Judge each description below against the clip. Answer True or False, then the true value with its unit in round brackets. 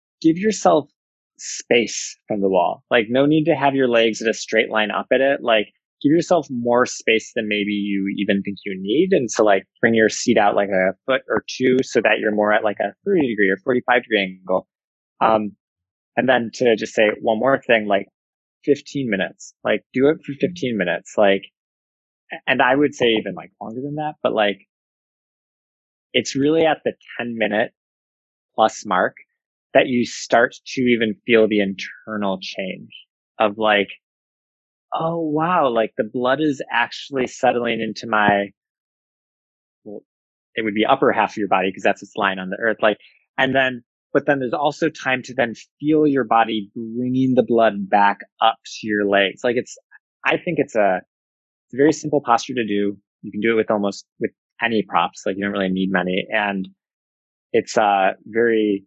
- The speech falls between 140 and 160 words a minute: False (190 wpm)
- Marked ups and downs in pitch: False (4.5 semitones)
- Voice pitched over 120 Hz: False (110 Hz)